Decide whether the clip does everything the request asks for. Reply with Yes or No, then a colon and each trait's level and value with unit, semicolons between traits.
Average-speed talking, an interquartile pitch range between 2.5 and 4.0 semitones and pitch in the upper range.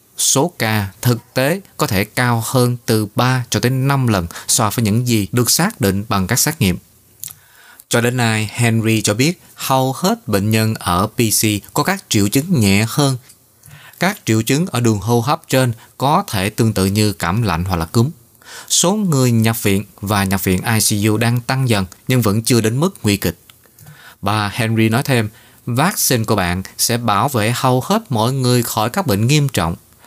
No: average, 195 wpm; average, 3.5 semitones; low, 115 Hz